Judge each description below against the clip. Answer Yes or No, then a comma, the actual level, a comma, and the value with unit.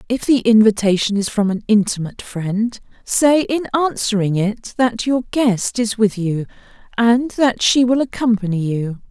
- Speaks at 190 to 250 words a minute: No, average, 160 wpm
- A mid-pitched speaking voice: No, high, 220 Hz